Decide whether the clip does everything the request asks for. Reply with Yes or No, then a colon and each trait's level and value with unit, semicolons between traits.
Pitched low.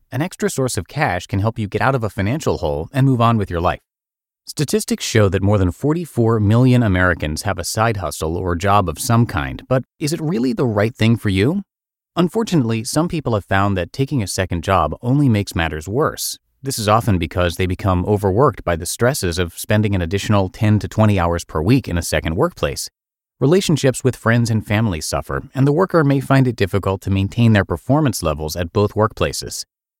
Yes: low, 105 Hz